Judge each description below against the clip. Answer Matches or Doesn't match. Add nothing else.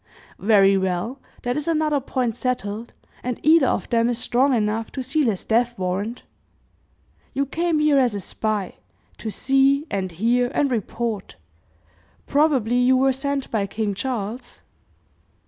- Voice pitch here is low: Doesn't match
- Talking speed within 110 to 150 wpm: Matches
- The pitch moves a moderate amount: Matches